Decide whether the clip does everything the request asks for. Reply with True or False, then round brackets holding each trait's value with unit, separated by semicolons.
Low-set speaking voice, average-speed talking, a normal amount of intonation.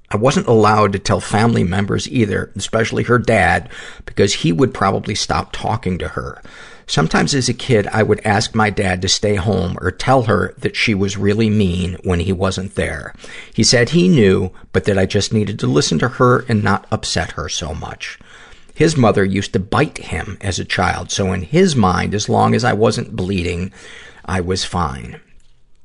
True (100 Hz; 195 wpm; 3.4 semitones)